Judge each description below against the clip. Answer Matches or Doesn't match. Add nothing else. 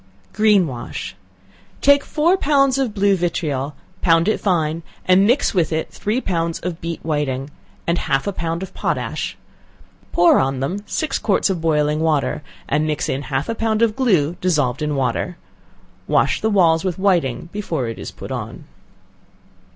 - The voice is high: Doesn't match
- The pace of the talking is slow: Doesn't match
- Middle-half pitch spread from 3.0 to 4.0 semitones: Doesn't match